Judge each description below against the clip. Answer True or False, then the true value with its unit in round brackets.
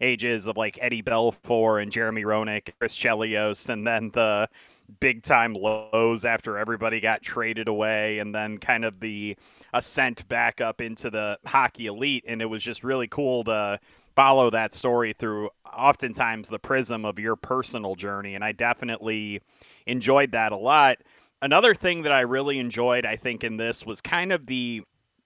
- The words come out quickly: False (170 wpm)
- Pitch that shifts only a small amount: True (2.3 semitones)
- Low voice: True (115 Hz)